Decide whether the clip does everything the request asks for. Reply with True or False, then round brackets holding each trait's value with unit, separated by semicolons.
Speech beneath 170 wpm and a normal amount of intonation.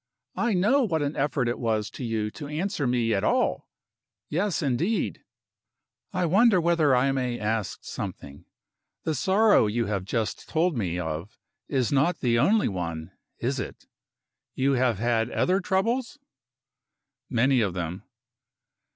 False (145 wpm; 8.0 semitones)